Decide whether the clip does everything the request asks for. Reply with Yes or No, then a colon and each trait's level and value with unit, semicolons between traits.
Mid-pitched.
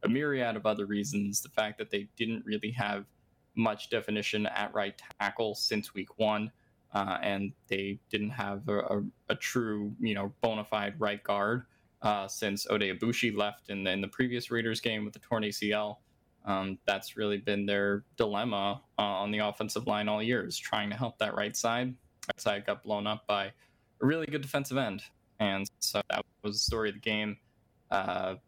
No: low, 105 Hz